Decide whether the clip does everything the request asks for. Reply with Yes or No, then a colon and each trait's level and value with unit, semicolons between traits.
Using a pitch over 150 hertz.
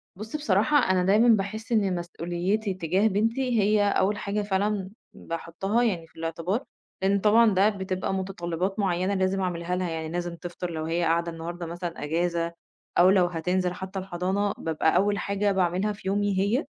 Yes: high, 190 Hz